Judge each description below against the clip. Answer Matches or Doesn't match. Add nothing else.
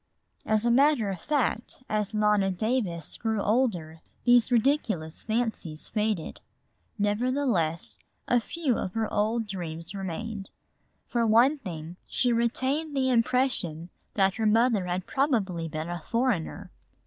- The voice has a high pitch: Matches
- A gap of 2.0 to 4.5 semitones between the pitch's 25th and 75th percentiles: Doesn't match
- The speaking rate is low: Matches